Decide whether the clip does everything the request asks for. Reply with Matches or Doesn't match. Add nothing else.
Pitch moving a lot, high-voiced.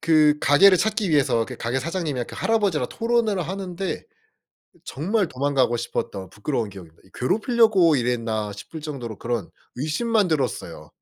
Doesn't match